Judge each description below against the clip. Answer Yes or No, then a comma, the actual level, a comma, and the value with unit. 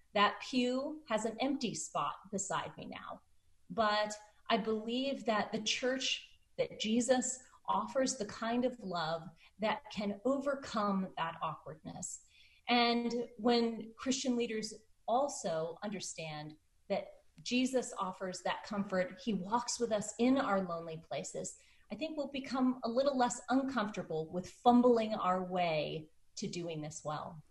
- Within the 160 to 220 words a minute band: No, slow, 135 wpm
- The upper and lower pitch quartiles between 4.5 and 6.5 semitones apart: Yes, average, 4.8 semitones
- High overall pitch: Yes, high, 220 Hz